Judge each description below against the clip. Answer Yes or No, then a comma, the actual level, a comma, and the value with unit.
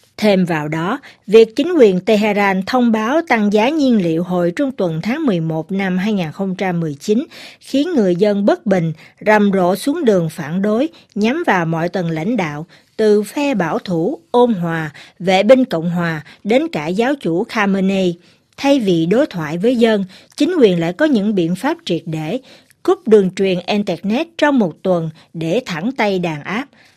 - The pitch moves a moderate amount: No, wide, 5.9 semitones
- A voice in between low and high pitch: No, high, 200 Hz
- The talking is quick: No, average, 175 wpm